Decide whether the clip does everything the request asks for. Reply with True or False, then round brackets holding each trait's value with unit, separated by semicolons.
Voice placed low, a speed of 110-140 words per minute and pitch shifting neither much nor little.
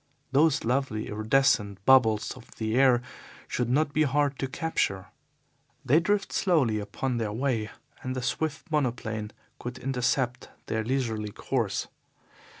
True (125 Hz; 135 wpm; 4.0 semitones)